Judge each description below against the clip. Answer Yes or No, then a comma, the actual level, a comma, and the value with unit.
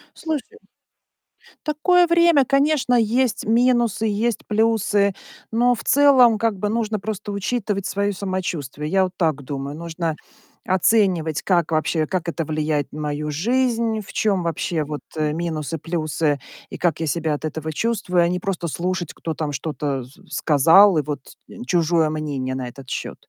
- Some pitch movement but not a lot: No, wide, 6.3 semitones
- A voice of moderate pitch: Yes, medium, 180 Hz